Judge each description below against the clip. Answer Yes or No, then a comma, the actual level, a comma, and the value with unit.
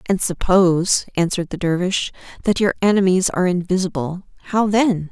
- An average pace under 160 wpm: Yes, average, 140 wpm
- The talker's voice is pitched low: No, medium, 185 Hz